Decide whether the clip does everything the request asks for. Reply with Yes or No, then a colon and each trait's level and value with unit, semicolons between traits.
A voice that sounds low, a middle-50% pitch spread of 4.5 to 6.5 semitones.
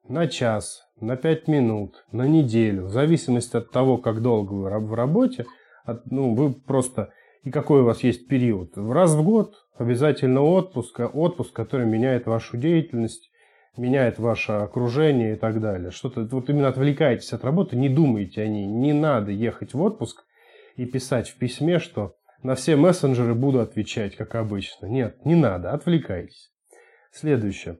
Yes: low, 125 Hz; average, 5.0 semitones